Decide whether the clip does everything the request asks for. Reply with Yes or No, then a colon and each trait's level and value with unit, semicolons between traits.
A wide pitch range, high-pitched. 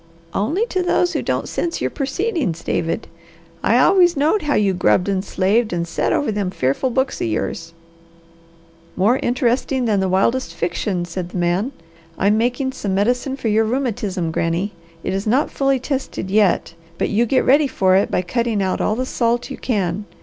Yes: wide, 5.9 semitones; high, 215 Hz